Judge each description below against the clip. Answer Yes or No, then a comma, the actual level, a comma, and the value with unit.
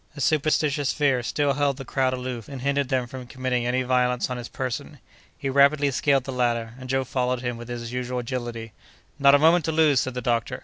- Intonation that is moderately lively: No, narrow, 2.3 semitones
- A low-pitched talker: Yes, low, 130 Hz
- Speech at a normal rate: No, fast, 220 wpm